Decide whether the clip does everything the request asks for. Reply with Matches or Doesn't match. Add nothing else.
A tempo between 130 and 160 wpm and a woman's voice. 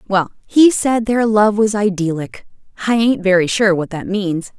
Doesn't match